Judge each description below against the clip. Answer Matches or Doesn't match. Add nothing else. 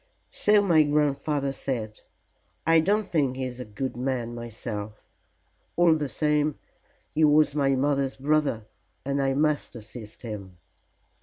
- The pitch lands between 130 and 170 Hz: Matches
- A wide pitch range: Doesn't match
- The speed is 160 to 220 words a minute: Doesn't match